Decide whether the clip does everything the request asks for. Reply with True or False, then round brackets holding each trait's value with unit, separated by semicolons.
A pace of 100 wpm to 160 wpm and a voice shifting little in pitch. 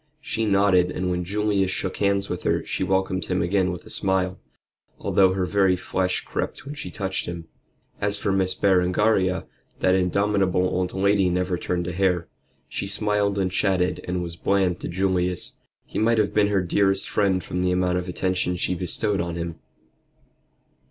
False (180 wpm; 1.6 semitones)